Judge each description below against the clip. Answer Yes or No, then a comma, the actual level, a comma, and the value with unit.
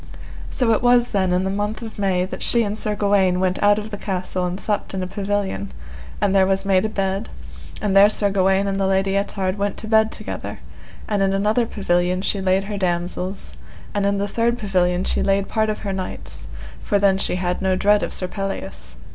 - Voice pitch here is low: No, high, 195 Hz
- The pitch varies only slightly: Yes, narrow, 1.7 semitones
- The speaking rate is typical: No, fast, 220 wpm